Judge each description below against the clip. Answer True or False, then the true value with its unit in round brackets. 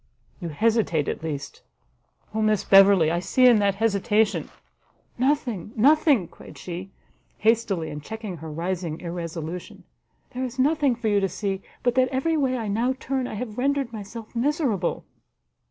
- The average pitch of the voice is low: False (215 Hz)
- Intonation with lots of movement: True (5.7 semitones)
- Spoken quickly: False (160 wpm)